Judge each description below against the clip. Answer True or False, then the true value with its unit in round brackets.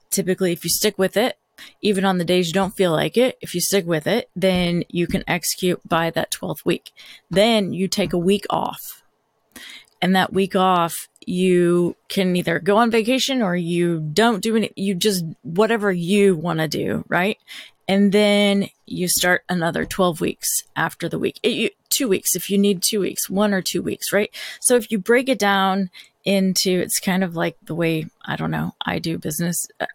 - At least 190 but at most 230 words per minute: True (200 wpm)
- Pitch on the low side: False (190 Hz)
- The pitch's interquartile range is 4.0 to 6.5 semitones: False (2.7 semitones)